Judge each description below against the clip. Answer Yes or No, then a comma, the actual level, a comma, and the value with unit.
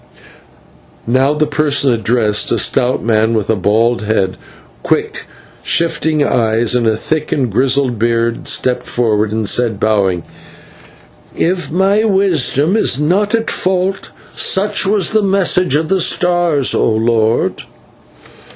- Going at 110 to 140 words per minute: Yes, slow, 135 wpm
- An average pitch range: No, wide, 7.9 semitones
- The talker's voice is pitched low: Yes, low, 130 Hz